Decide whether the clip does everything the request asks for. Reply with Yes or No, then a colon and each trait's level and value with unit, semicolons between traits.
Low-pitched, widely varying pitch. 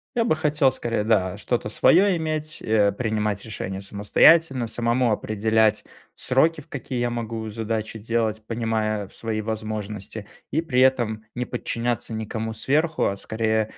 No: low, 115 Hz; average, 2.9 semitones